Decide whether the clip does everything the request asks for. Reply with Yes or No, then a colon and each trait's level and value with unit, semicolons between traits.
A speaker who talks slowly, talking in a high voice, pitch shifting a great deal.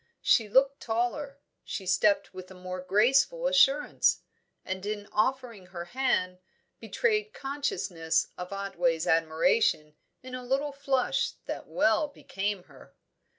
Yes: slow, 125 wpm; high, 220 Hz; wide, 7.1 semitones